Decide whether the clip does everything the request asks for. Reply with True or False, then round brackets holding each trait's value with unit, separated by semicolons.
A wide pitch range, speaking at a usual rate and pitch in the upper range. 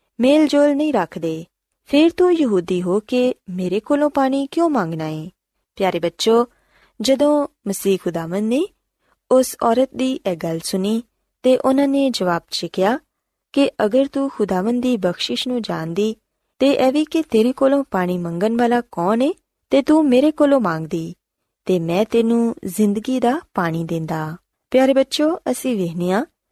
True (6.7 semitones; 145 wpm; 235 Hz)